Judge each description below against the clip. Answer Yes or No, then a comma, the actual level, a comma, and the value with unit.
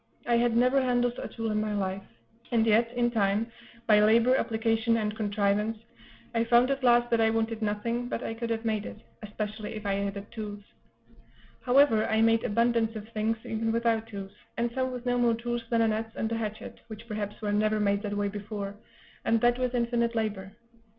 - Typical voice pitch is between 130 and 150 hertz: No, high, 225 Hz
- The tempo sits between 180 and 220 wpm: Yes, fast, 205 wpm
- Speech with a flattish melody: Yes, narrow, 2.0 semitones